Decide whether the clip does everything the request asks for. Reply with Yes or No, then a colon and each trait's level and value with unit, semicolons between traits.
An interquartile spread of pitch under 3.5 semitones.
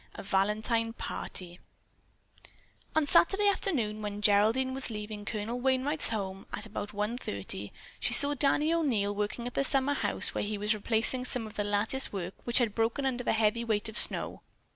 No: average, 4.0 semitones